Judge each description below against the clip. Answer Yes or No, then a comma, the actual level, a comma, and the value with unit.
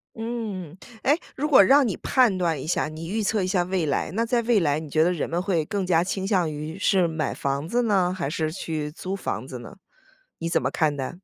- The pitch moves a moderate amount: Yes, average, 4.6 semitones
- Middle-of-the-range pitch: Yes, medium, 180 Hz